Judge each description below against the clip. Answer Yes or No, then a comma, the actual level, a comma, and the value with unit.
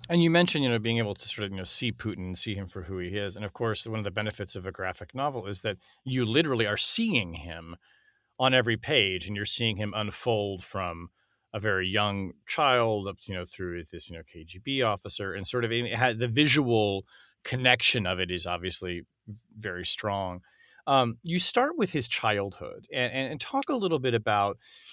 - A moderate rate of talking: No, fast, 210 wpm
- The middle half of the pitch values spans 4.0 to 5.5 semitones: Yes, average, 4.7 semitones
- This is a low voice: Yes, low, 105 Hz